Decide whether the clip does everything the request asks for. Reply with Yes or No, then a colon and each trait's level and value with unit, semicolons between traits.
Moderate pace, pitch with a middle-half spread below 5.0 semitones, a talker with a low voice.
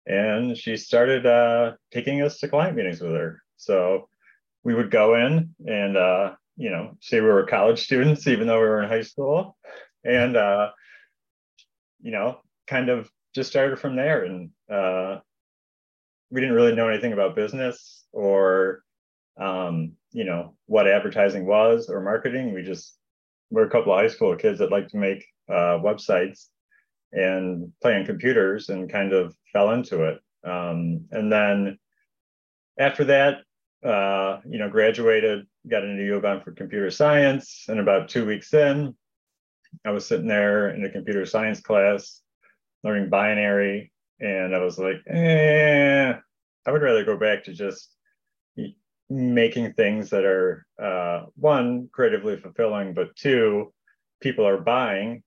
No: average, 150 wpm; wide, 5.5 semitones; low, 110 Hz